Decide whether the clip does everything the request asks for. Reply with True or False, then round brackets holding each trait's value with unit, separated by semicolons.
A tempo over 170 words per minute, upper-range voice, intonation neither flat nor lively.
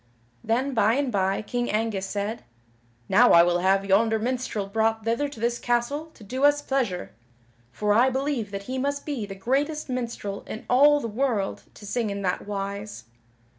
True (180 wpm; 225 Hz; 4.4 semitones)